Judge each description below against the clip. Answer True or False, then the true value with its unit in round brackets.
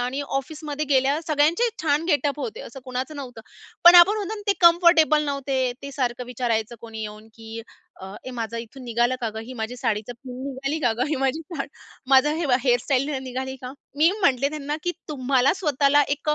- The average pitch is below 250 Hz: False (270 Hz)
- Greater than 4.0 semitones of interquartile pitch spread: False (3.5 semitones)